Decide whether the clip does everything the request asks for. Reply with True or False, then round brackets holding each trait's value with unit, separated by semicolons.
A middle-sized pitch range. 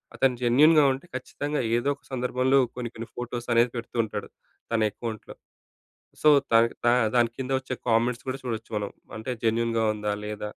False (2.2 semitones)